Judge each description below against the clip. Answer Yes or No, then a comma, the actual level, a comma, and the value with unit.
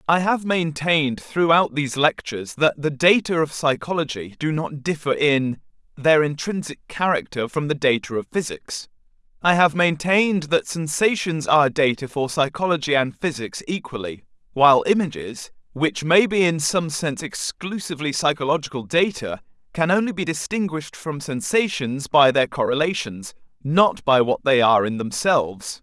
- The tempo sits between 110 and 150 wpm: Yes, average, 145 wpm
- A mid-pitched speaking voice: Yes, medium, 150 Hz